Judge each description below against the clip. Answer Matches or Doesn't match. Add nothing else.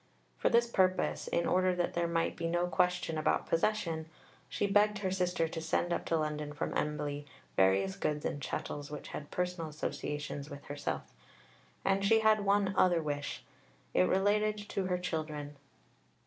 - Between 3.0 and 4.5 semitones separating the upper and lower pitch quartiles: Matches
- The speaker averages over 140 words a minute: Matches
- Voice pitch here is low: Doesn't match